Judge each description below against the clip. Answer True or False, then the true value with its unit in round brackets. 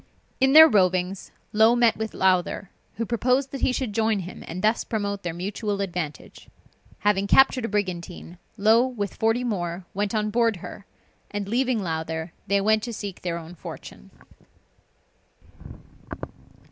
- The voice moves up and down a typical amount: True (3.9 semitones)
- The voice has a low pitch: False (205 Hz)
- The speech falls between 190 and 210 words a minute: False (150 wpm)